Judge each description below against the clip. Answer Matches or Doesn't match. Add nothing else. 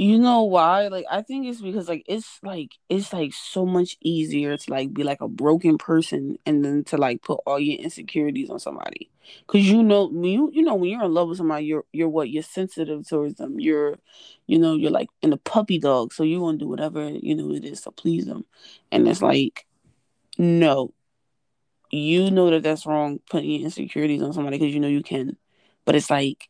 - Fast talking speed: Matches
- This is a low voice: Doesn't match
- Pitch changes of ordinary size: Doesn't match